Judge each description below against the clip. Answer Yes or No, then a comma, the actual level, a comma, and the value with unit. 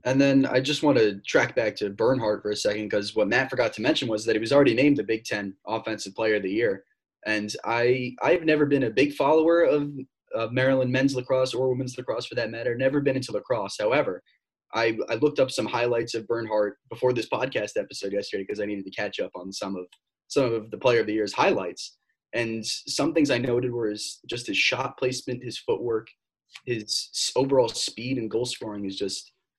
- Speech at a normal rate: No, fast, 220 wpm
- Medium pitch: No, low, 120 Hz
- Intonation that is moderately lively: Yes, average, 4.1 semitones